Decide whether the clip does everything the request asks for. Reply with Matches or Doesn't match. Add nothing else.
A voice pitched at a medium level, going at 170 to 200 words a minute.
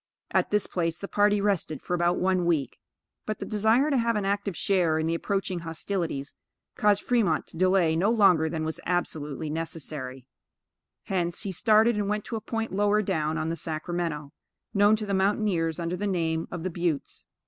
Matches